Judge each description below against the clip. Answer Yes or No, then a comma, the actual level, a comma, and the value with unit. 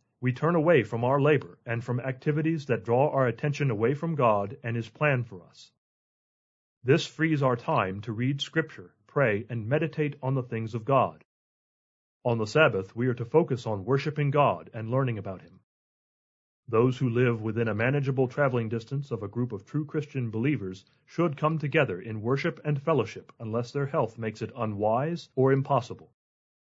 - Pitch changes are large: No, average, 4.4 semitones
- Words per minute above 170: Yes, average, 180 wpm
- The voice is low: Yes, low, 130 Hz